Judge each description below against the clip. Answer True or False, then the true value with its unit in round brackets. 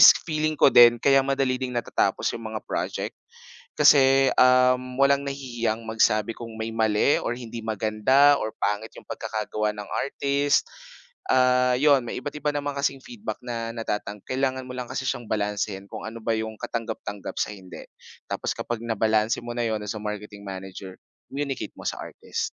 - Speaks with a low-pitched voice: True (120 Hz)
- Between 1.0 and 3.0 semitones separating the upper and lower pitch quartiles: False (3.8 semitones)